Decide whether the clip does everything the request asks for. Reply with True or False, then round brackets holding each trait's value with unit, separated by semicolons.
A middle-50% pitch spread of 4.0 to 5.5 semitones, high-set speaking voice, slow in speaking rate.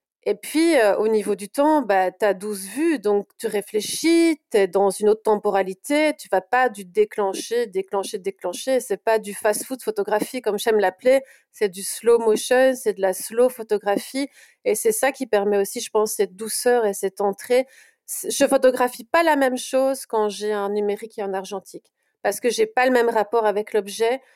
False (4.5 semitones; 220 Hz; 195 wpm)